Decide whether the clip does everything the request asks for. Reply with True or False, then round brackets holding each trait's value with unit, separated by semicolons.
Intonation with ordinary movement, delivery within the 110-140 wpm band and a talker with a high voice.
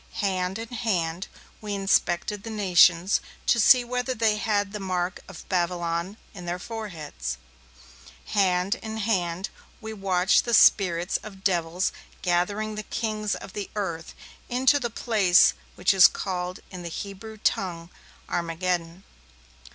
True (3.4 semitones; 135 wpm; 195 Hz)